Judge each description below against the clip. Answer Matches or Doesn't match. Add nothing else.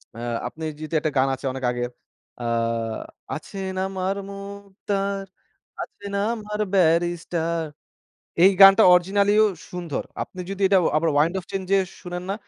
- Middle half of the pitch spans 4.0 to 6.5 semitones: Doesn't match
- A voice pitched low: Doesn't match